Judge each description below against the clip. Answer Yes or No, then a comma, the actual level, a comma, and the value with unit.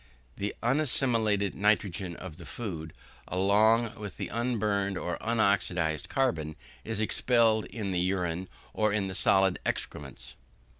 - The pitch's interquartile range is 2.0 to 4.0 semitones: Yes, average, 3.5 semitones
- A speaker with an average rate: No, slow, 130 wpm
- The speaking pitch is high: No, low, 100 Hz